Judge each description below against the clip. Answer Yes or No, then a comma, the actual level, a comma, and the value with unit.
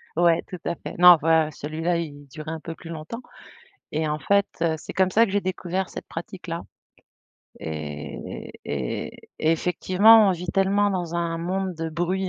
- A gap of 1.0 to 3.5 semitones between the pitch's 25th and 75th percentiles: Yes, average, 2.9 semitones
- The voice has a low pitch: No, medium, 170 Hz